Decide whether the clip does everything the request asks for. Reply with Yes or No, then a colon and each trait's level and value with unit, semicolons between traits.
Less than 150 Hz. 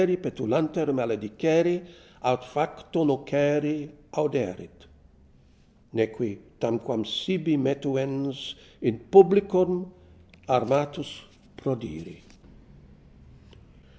Yes: medium, 140 Hz